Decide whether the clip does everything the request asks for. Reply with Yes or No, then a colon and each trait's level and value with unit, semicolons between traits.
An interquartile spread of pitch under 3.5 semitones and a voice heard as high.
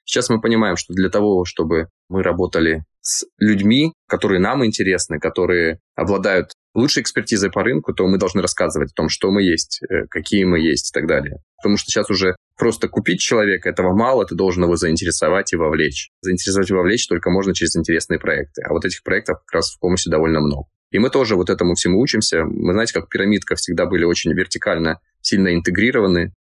No: narrow, 2.5 semitones; very low, 90 Hz